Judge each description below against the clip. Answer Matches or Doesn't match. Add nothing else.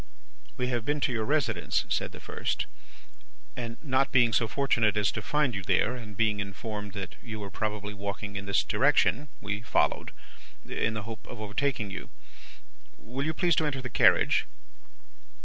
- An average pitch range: Matches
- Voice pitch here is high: Doesn't match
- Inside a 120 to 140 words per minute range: Doesn't match